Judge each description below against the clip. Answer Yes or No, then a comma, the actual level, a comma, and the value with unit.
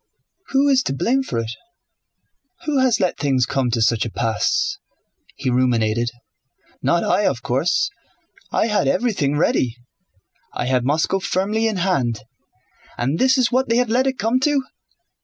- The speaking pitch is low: No, medium, 175 Hz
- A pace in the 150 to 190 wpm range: Yes, average, 160 wpm